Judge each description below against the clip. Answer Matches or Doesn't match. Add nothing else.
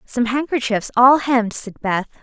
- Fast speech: Doesn't match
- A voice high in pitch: Matches